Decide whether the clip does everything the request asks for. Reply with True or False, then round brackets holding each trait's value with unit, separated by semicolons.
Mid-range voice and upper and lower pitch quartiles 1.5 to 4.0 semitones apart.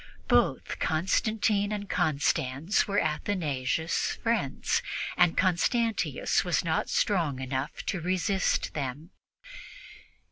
False (175 Hz; 5.5 semitones)